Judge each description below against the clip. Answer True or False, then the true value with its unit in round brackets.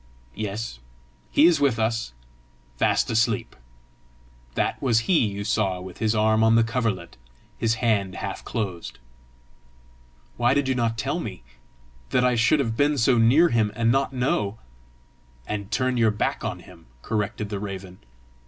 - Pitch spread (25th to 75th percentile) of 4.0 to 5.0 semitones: False (3.1 semitones)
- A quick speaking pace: False (155 wpm)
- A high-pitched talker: False (115 Hz)